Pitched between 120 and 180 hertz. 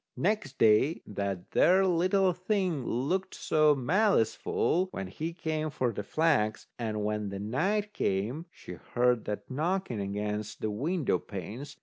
Yes: medium, 140 Hz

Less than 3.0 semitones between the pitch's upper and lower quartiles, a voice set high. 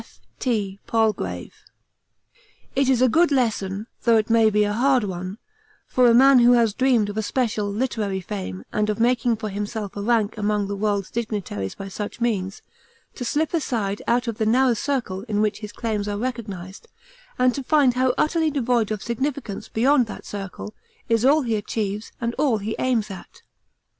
No: average, 3.4 semitones; high, 220 Hz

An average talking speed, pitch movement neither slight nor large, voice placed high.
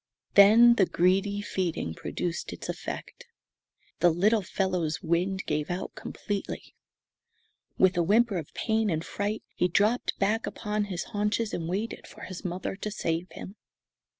Yes: average, 150 wpm; average, 3.1 semitones; high, 195 Hz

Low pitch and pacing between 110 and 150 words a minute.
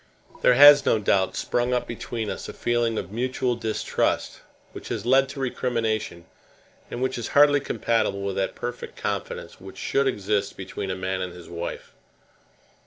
No: low, 115 Hz; average, 170 wpm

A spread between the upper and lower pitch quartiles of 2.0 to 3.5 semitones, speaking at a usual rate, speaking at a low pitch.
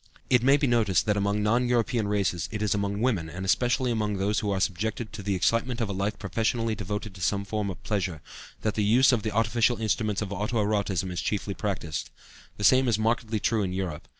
No: narrow, 2.5 semitones; fast, 225 wpm; low, 105 Hz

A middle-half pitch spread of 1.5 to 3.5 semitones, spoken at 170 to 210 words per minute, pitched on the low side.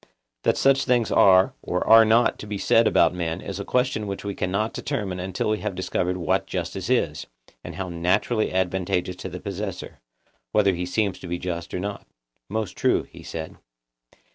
Yes: average, 3.1 semitones; average, 190 wpm; very low, 95 Hz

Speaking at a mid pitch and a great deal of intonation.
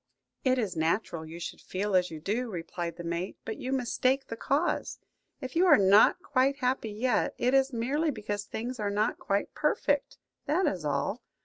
No: high, 225 Hz; wide, 6.0 semitones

